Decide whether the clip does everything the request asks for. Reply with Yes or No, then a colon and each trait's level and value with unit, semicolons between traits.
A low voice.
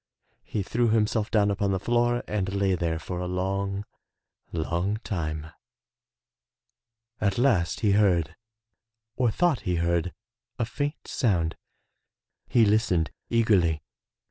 Yes: low, 100 Hz